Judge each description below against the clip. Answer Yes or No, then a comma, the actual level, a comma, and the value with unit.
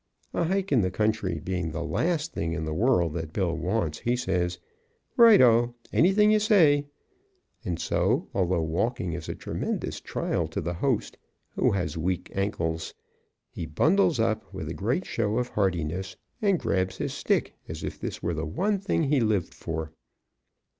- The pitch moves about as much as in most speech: No, wide, 8.7 semitones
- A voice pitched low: Yes, low, 100 Hz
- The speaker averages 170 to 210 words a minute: Yes, average, 175 wpm